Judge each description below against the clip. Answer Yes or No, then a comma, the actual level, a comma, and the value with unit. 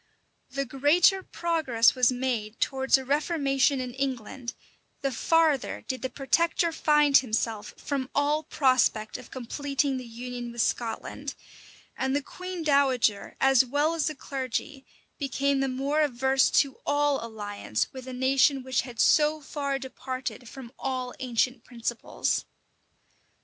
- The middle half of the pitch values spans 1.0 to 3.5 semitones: Yes, narrow, 2.5 semitones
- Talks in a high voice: Yes, very high, 265 Hz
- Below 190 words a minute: Yes, average, 140 wpm